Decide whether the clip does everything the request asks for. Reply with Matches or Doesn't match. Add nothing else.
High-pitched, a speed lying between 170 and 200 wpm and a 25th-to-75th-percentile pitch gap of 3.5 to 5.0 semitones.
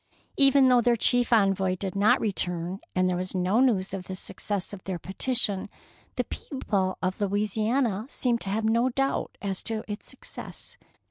Matches